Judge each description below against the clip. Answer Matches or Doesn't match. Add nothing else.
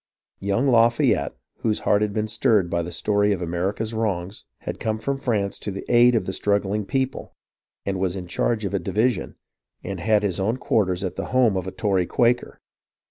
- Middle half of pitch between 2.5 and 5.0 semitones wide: Matches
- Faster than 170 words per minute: Matches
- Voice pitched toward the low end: Matches